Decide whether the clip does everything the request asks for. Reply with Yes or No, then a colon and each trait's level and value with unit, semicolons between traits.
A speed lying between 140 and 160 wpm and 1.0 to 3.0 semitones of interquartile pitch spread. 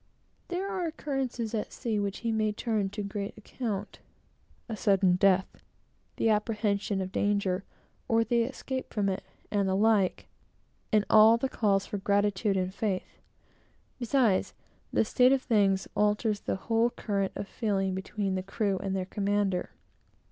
Yes: average, 155 wpm; narrow, 2.6 semitones